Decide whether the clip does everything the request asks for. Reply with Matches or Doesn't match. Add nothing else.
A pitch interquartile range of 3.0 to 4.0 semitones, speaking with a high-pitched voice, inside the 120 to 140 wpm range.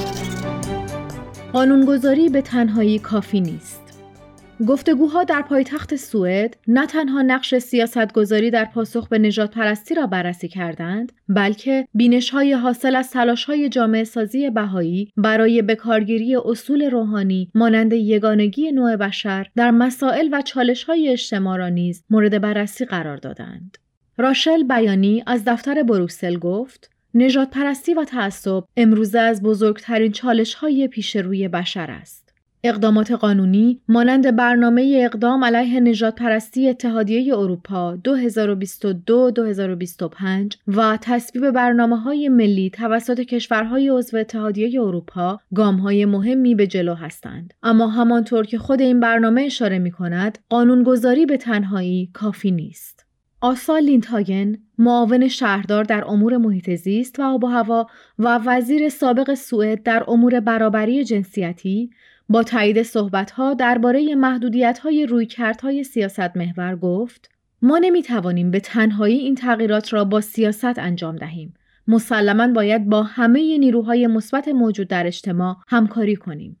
Matches